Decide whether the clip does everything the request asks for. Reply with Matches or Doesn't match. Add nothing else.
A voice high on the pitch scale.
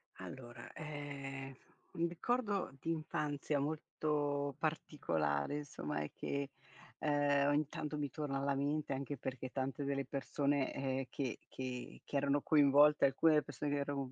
Doesn't match